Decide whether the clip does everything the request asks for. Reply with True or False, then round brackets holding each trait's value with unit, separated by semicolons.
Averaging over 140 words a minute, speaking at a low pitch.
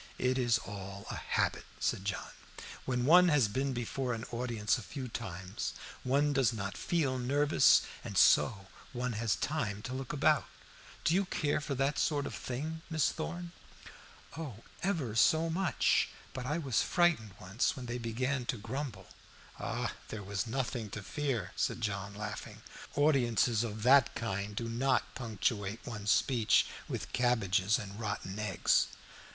True (155 wpm; 120 Hz)